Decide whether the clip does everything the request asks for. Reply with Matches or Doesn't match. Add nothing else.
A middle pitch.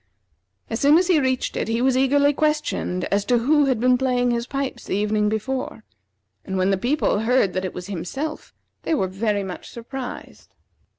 Doesn't match